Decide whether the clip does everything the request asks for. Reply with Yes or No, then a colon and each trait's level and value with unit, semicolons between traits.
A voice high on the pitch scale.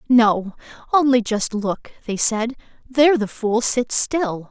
Yes: high, 235 Hz